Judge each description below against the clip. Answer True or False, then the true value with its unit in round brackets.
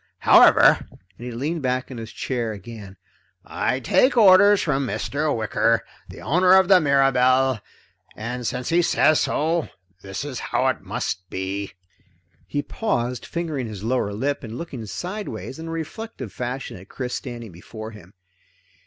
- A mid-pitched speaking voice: False (130 Hz)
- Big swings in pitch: True (6.1 semitones)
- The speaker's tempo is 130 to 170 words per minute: True (155 wpm)